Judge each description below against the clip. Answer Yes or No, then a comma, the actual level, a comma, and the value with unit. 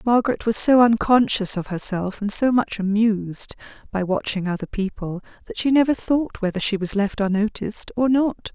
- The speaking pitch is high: Yes, high, 215 Hz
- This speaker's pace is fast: No, average, 175 wpm